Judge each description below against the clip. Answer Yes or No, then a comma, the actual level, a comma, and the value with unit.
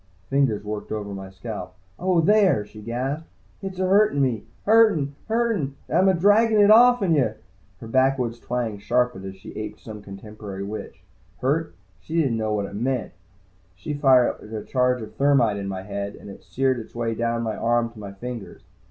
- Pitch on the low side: Yes, low, 120 Hz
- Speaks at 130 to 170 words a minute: No, average, 185 wpm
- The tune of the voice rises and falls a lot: Yes, wide, 6.0 semitones